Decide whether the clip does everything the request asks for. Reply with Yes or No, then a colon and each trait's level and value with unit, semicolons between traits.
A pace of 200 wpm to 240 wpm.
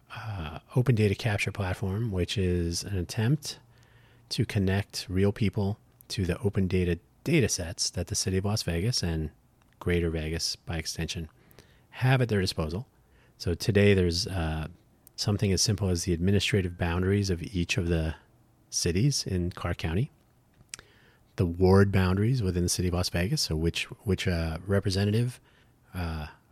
No: average, 155 wpm